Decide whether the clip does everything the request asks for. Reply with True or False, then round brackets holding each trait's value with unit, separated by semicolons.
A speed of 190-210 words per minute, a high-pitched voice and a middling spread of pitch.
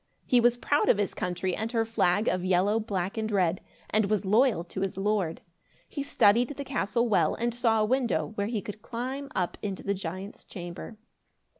True (195 wpm; 210 Hz; 3.9 semitones)